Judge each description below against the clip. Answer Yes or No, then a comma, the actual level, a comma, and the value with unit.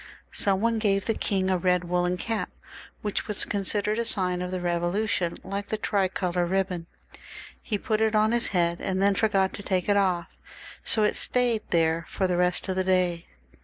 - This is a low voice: No, high, 190 Hz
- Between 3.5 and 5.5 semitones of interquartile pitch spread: No, average, 2.8 semitones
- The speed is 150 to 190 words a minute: No, average, 200 wpm